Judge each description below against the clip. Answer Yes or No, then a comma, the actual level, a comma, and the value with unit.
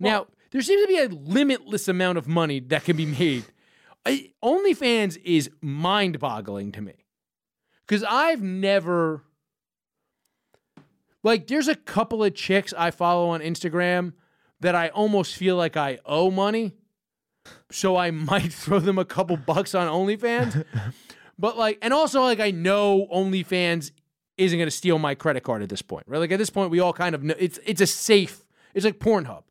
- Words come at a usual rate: Yes, average, 175 wpm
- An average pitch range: Yes, average, 4.1 semitones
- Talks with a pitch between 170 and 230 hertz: Yes, medium, 185 Hz